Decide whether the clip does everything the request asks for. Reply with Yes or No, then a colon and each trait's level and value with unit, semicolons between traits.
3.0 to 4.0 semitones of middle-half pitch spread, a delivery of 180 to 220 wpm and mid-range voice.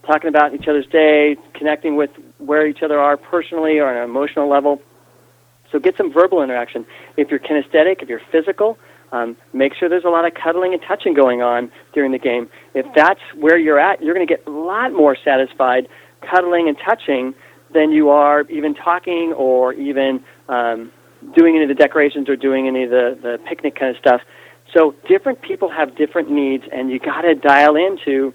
Yes: average, 3.5 semitones; average, 200 wpm; medium, 145 Hz